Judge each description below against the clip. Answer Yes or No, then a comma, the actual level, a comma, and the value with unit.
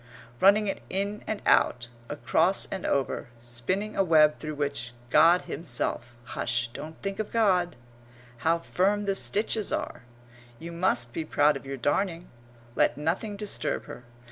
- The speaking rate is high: No, average, 150 wpm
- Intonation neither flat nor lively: No, wide, 6.0 semitones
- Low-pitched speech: No, medium, 165 Hz